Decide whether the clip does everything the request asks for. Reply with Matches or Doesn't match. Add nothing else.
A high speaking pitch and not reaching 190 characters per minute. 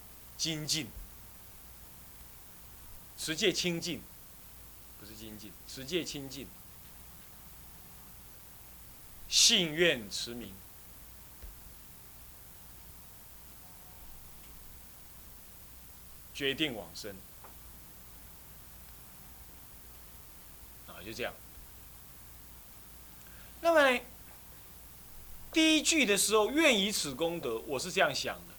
Doesn't match